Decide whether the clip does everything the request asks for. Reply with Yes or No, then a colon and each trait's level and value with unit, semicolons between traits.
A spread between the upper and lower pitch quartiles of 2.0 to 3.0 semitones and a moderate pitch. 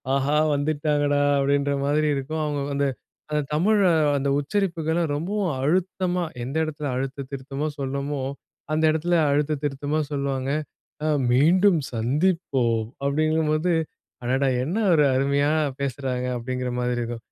Yes: narrow, 2.5 semitones; medium, 145 Hz